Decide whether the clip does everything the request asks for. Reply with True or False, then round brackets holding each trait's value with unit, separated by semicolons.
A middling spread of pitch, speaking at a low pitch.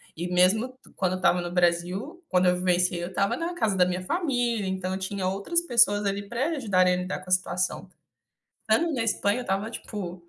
False (4.4 semitones; 190 Hz)